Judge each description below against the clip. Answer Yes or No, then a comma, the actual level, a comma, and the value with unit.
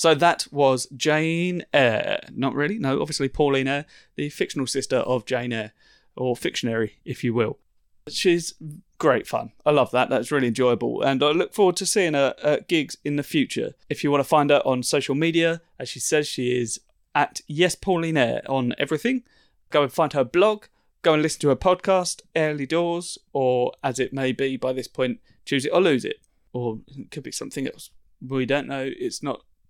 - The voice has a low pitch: No, medium, 145 Hz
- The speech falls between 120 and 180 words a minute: No, average, 200 wpm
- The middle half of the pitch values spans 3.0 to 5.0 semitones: Yes, average, 4.3 semitones